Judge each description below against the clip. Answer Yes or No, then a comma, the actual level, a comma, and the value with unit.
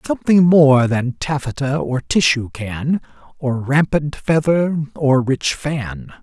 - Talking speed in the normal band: No, slow, 125 wpm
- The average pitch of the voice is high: No, medium, 140 Hz